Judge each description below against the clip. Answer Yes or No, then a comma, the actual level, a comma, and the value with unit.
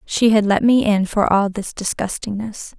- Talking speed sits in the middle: Yes, average, 195 wpm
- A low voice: No, high, 210 Hz